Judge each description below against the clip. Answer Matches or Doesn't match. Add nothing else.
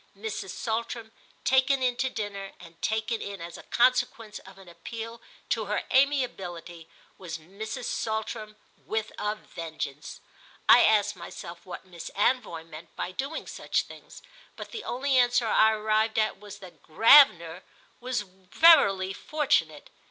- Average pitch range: Matches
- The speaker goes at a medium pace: Matches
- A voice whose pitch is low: Doesn't match